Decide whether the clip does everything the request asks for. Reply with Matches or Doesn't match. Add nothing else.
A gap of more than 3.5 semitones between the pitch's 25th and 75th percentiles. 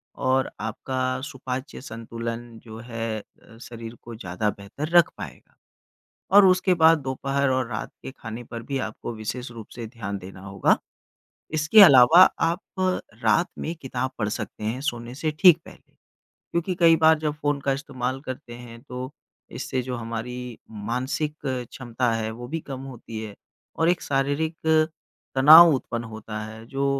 Matches